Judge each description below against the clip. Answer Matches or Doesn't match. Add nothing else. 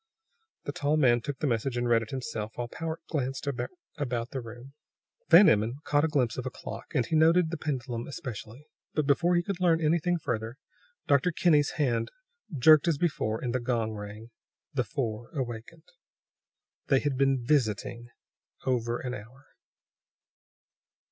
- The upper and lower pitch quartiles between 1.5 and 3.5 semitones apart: Doesn't match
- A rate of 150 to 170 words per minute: Matches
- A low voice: Matches